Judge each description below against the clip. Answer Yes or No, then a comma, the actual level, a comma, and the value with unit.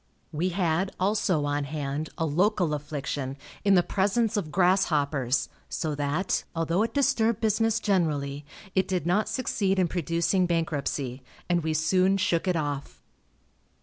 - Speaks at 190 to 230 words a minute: No, average, 145 wpm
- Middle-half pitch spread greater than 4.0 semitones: Yes, average, 4.6 semitones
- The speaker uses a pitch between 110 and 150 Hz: No, medium, 170 Hz